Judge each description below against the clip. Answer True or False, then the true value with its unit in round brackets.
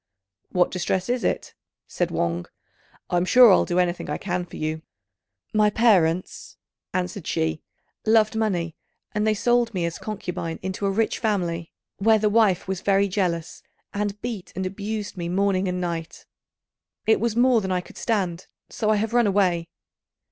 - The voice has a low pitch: False (190 Hz)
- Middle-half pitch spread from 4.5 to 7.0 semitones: False (3.6 semitones)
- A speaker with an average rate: True (170 wpm)